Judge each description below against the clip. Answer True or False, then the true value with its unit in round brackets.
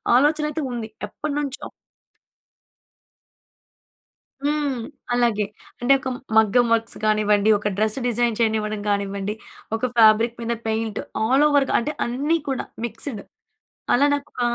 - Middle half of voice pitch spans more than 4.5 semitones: False (4.1 semitones)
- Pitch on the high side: True (235 Hz)